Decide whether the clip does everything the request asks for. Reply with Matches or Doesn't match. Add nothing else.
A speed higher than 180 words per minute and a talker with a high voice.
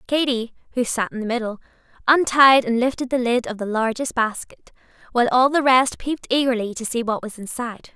Matches